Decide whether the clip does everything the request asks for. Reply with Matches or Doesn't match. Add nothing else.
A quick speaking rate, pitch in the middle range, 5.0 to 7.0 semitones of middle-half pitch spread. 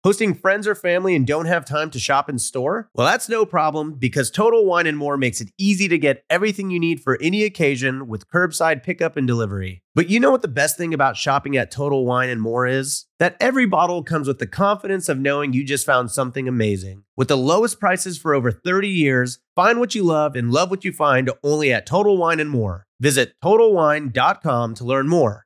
Matches